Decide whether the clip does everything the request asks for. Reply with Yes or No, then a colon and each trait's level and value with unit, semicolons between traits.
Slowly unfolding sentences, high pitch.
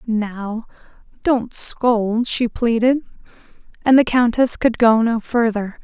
Yes: slow, 125 wpm; high, 230 Hz